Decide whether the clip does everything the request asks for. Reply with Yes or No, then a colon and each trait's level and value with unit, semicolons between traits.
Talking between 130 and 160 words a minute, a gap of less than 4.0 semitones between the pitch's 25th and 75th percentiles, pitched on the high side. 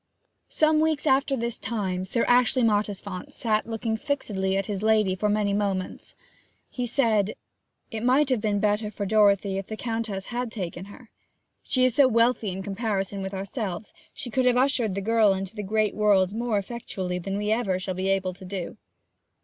No: average, 185 wpm; average, 3.4 semitones; high, 210 Hz